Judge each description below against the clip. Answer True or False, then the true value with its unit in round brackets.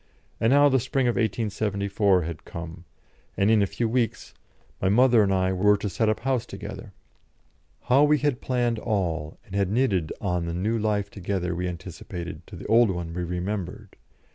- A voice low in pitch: True (100 Hz)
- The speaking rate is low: False (185 wpm)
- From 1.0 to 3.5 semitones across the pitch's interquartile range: False (4.4 semitones)